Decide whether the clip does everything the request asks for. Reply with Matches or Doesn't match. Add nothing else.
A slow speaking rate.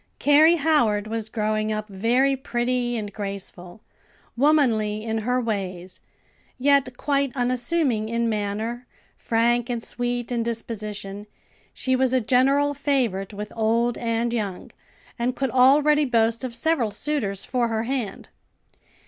Matches